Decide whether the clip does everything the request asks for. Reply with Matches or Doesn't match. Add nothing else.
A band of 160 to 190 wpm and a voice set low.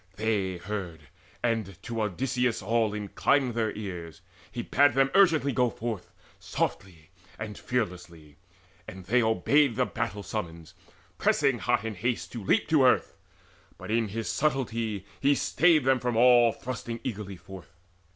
Doesn't match